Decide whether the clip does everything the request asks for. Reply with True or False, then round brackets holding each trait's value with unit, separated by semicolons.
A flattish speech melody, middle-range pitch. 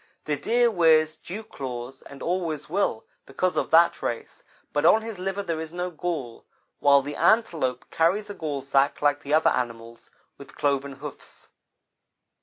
False (4.5 semitones; 155 Hz)